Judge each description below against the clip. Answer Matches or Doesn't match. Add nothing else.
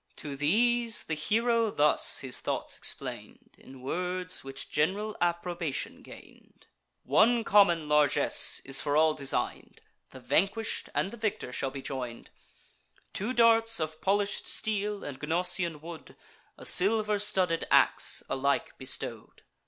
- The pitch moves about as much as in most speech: Doesn't match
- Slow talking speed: Matches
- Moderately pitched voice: Matches